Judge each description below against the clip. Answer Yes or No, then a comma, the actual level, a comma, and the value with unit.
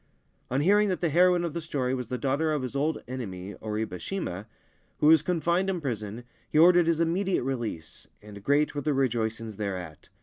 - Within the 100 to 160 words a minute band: No, average, 195 wpm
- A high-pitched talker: No, low, 135 Hz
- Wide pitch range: Yes, wide, 7.1 semitones